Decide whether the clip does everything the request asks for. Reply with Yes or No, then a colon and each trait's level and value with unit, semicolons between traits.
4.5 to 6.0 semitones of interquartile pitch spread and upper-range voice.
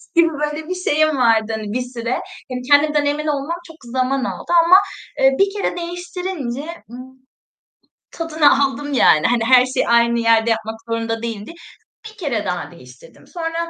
Yes: average, 5.1 semitones; very high, 265 Hz